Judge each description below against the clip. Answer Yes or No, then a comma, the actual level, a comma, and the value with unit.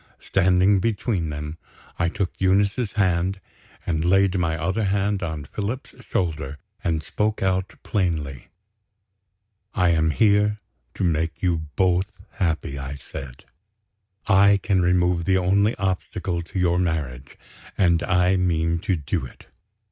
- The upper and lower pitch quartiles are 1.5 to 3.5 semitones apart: Yes, average, 3.1 semitones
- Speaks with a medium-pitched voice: No, very low, 90 Hz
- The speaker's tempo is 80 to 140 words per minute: Yes, slow, 135 wpm